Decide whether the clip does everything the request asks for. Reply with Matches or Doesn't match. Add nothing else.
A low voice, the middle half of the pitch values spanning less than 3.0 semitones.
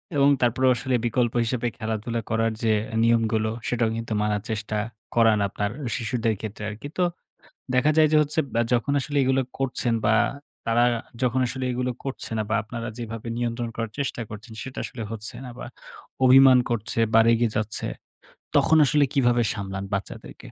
Matches